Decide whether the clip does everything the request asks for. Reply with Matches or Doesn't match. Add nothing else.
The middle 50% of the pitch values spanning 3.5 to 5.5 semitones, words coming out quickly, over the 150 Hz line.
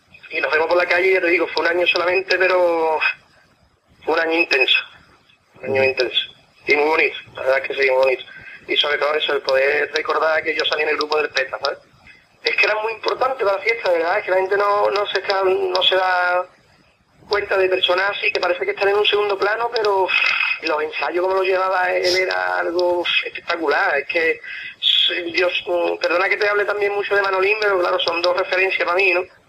Doesn't match